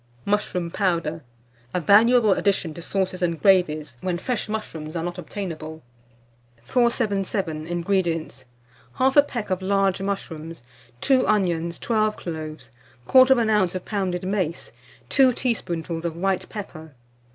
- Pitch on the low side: No, medium, 185 Hz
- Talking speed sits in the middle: No, slow, 125 wpm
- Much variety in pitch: No, average, 4.0 semitones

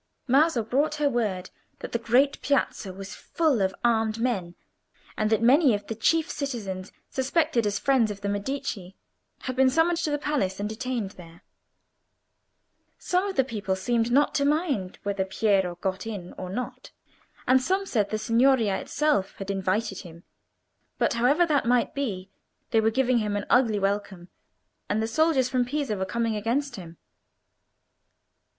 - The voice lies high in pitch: Yes, high, 230 Hz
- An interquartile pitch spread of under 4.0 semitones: No, average, 5.3 semitones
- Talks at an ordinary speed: Yes, average, 165 wpm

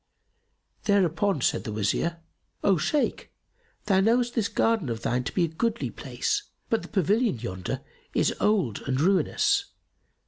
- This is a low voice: No, high, 195 Hz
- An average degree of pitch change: No, wide, 8.3 semitones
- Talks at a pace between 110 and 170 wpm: Yes, average, 145 wpm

